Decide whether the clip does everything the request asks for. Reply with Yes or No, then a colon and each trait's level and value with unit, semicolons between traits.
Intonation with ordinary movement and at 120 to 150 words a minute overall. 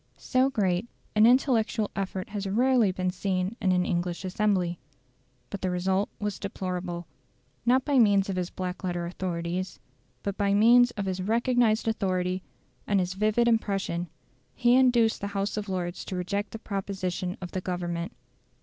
No: average, 3.0 semitones; average, 160 wpm